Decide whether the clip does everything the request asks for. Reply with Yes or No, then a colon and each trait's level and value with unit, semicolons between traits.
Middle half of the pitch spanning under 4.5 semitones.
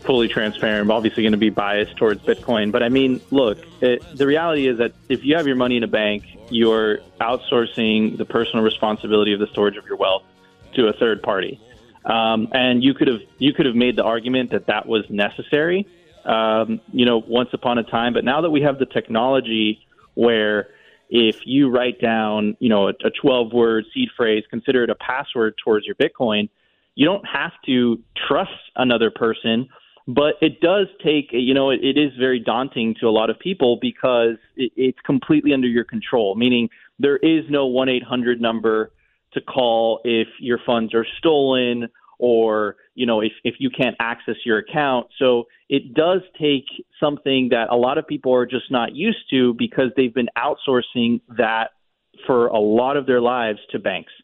Yes: average, 2.8 semitones